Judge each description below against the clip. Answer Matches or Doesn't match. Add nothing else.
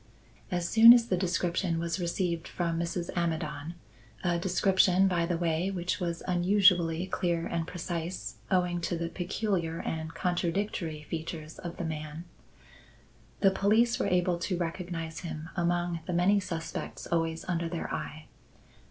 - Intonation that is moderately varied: Doesn't match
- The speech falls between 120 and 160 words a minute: Matches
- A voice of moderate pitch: Matches